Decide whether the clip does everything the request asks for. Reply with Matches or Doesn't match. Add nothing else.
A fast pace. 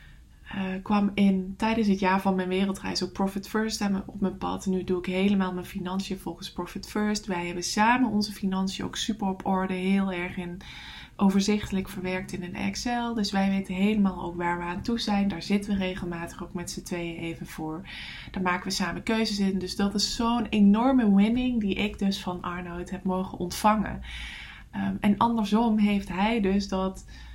Doesn't match